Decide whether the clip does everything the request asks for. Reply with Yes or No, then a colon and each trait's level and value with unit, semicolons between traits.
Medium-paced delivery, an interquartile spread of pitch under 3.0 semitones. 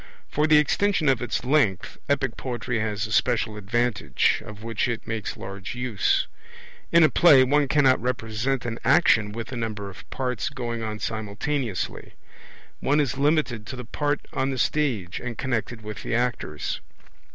No: average, 165 wpm; average, 3.8 semitones